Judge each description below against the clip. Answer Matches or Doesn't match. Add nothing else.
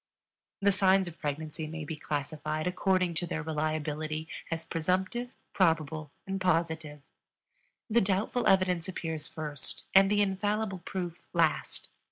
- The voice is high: Doesn't match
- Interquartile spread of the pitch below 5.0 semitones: Matches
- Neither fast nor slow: Doesn't match